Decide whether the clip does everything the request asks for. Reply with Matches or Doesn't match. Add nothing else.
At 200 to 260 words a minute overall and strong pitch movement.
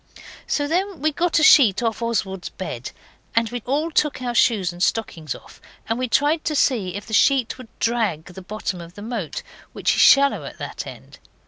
Matches